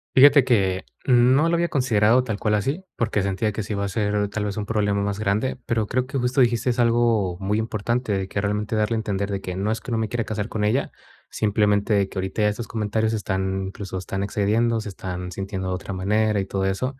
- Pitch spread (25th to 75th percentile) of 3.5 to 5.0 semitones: No, average, 2.8 semitones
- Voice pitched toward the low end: Yes, low, 105 Hz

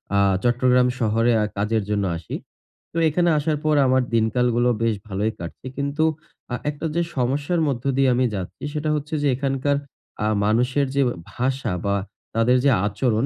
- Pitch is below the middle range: Yes, low, 125 Hz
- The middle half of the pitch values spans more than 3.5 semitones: Yes, average, 4.0 semitones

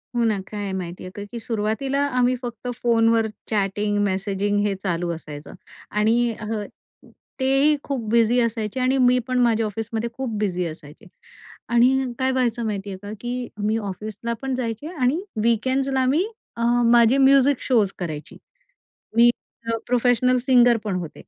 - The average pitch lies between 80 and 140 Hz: No, high, 230 Hz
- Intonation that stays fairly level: No, average, 3.4 semitones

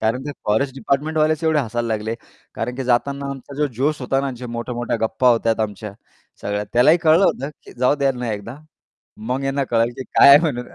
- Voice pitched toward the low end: Yes, low, 125 Hz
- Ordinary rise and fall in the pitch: Yes, average, 3.2 semitones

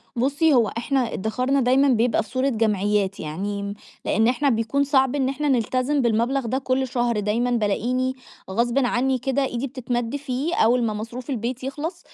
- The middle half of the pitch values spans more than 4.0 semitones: No, average, 2.9 semitones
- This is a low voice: No, very high, 250 Hz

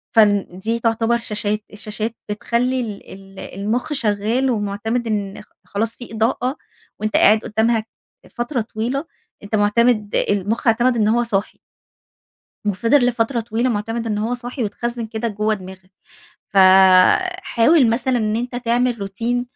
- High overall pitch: Yes, high, 225 Hz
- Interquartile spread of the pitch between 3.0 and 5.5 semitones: No, narrow, 2.4 semitones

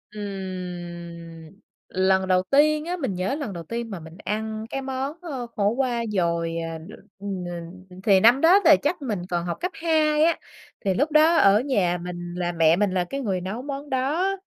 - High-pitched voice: Yes, high, 215 Hz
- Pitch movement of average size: No, wide, 7.9 semitones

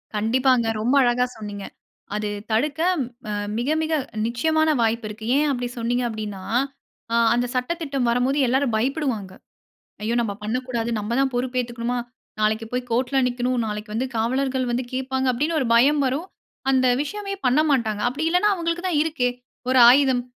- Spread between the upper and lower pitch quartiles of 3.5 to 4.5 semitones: No, average, 2.9 semitones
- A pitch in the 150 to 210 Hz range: No, very high, 250 Hz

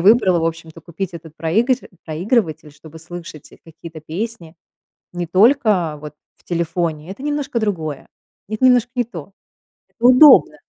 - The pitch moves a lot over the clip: Yes, wide, 6.1 semitones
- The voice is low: No, medium, 175 Hz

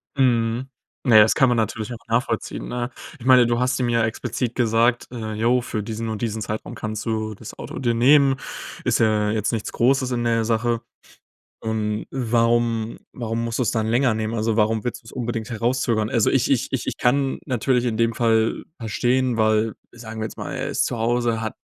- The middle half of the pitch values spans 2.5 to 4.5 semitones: No, narrow, 1.7 semitones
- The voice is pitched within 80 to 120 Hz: Yes, low, 115 Hz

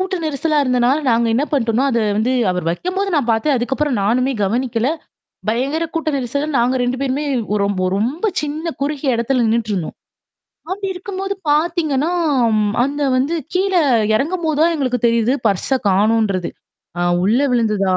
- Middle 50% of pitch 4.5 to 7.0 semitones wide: Yes, average, 5.1 semitones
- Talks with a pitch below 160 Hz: No, very high, 260 Hz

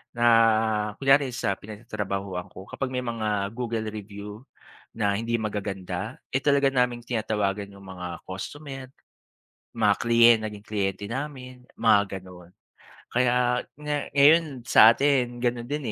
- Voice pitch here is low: Yes, low, 115 Hz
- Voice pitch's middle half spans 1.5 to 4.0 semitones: Yes, average, 3.7 semitones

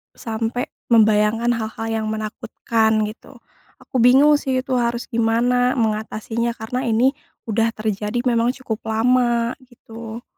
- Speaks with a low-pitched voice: No, high, 230 Hz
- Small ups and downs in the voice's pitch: Yes, narrow, 1.9 semitones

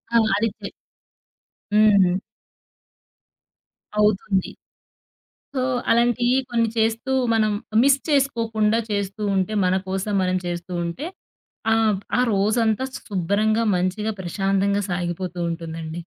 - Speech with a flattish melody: No, average, 3.4 semitones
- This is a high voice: Yes, high, 205 Hz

